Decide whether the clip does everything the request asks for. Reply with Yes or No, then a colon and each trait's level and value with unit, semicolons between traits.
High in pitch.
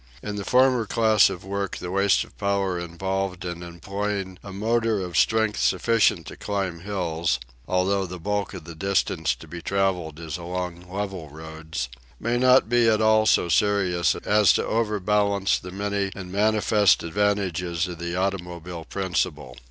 No: very low, 95 Hz